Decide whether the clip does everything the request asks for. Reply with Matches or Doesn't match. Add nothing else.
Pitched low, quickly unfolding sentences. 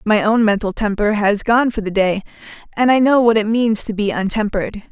Doesn't match